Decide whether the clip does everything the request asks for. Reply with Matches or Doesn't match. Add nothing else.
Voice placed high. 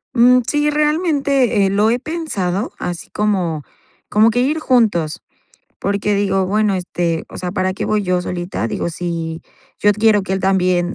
Matches